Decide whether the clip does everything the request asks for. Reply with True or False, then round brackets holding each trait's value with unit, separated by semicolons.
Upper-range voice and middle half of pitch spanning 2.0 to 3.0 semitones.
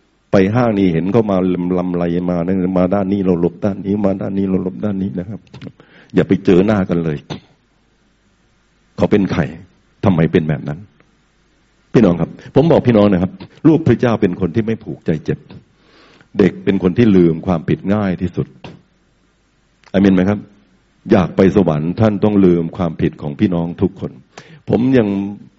False (95 Hz; 2.5 semitones)